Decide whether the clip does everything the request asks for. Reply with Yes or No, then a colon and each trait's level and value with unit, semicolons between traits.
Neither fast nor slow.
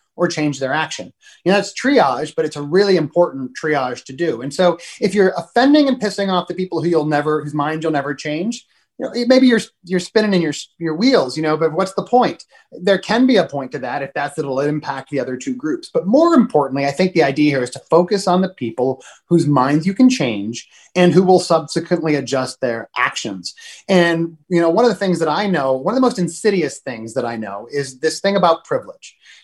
No: fast, 235 wpm